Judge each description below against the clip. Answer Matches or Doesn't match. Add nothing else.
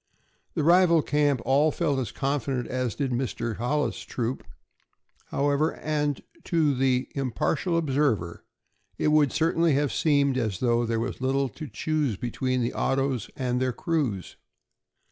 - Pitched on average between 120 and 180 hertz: Matches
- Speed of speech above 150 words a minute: Doesn't match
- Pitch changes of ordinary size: Matches